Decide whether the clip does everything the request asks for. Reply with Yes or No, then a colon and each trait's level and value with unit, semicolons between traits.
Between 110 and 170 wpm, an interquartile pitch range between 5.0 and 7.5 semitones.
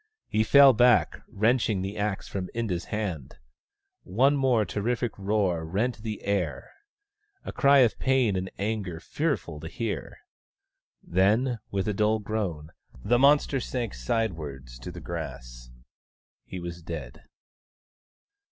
Yes: slow, 135 wpm; wide, 5.6 semitones